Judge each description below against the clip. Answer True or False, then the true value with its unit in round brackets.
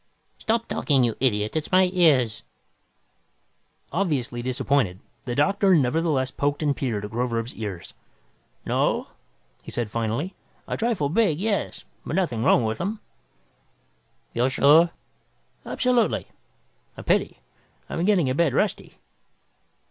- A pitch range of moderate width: False (6.8 semitones)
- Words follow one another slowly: True (125 wpm)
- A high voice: False (140 Hz)